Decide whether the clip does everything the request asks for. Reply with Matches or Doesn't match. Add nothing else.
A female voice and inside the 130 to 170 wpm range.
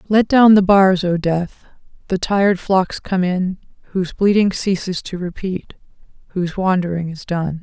Matches